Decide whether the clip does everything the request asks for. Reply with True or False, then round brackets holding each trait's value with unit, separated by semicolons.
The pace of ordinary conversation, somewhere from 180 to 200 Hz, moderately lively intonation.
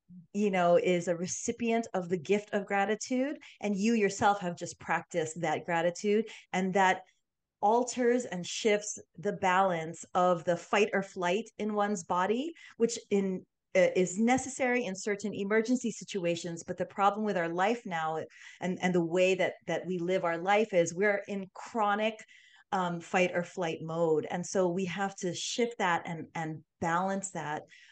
True (170 wpm; 190 Hz; 3.1 semitones)